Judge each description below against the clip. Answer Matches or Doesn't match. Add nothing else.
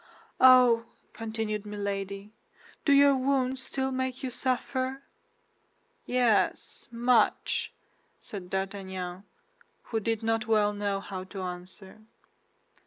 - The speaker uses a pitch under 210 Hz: Doesn't match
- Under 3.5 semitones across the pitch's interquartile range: Doesn't match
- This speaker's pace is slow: Matches